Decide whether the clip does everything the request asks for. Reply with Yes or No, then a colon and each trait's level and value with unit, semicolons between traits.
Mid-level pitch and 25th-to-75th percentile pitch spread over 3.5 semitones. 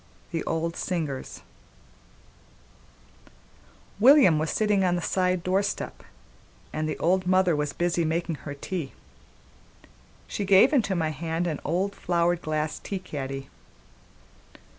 No: medium, 175 Hz; average, 3.2 semitones